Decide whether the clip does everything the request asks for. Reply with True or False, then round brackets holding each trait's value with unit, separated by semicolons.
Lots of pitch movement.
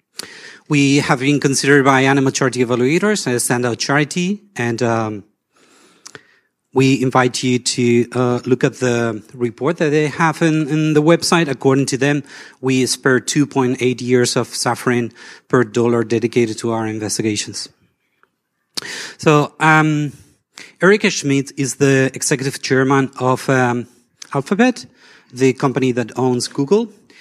False (3.2 semitones)